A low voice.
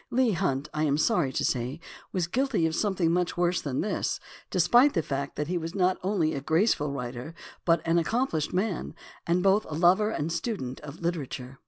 No: medium, 170 Hz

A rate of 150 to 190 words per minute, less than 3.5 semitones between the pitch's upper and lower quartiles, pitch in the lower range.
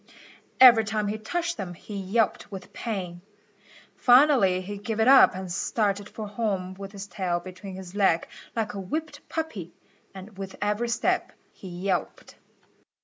No: average, 155 wpm; average, 3.1 semitones; high, 200 Hz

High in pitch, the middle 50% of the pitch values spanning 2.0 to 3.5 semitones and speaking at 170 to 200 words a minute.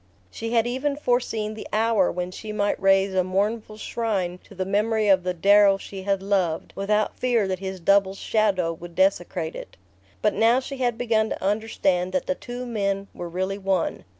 Yes: high, 200 Hz; average, 2.9 semitones; average, 190 wpm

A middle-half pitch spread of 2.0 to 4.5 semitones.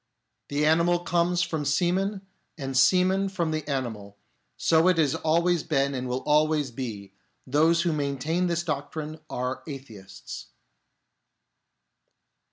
Yes: average, 4.0 semitones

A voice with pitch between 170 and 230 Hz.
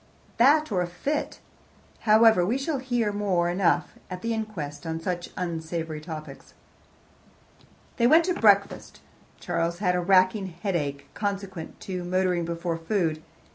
Yes: medium, 185 Hz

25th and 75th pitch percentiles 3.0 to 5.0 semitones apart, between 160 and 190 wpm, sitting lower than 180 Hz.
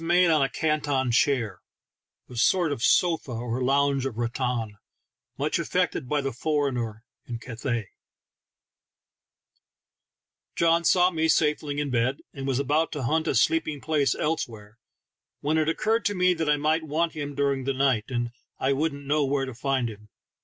Yes: average, 4.0 semitones; average, 165 wpm; medium, 140 Hz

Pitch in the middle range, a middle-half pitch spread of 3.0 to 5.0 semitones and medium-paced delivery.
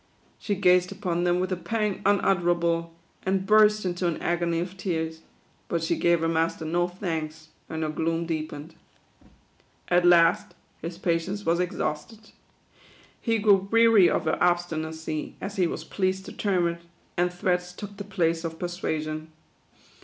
No: medium, 175 Hz; narrow, 2.6 semitones; average, 170 wpm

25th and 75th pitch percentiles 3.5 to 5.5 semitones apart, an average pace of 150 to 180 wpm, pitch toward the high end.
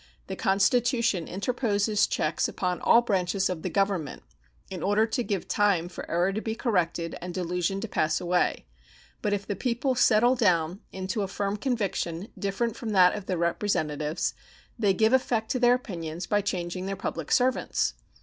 Yes: average, 3.8 semitones; average, 170 wpm; high, 195 Hz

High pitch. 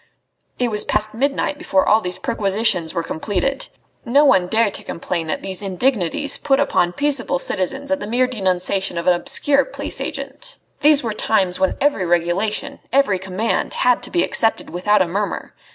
Yes: high, 210 Hz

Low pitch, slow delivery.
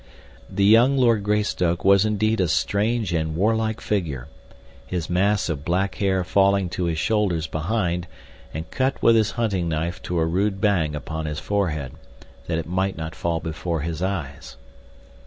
No: very low, 90 Hz; average, 170 wpm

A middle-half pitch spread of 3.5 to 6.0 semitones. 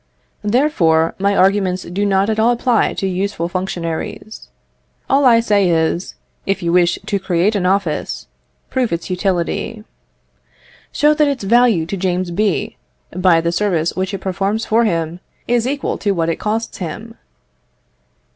Yes: average, 4.0 semitones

